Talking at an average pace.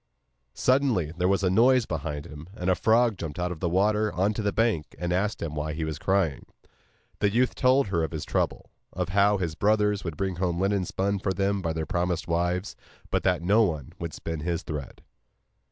No: fast, 220 wpm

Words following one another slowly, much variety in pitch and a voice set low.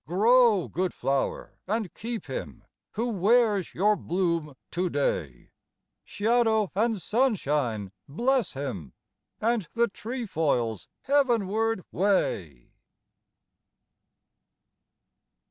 No: slow, 80 wpm; wide, 7.8 semitones; high, 195 Hz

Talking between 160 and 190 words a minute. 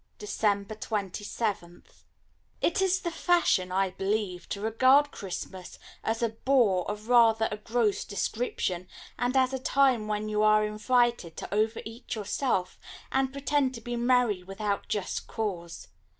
No: average, 145 wpm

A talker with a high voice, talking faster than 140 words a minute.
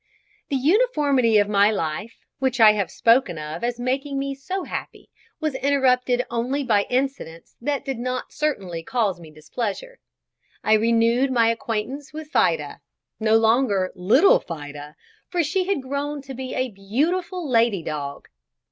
Yes: high, 245 Hz; average, 150 wpm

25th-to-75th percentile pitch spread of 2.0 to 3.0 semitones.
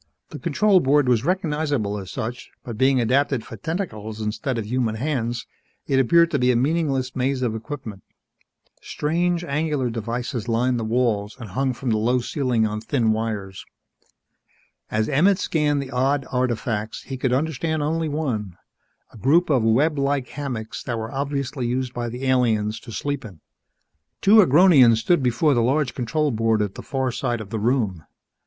No: average, 4.3 semitones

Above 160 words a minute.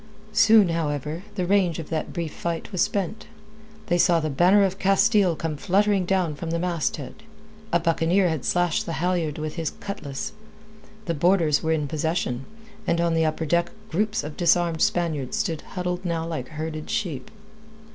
Yes: average, 170 wpm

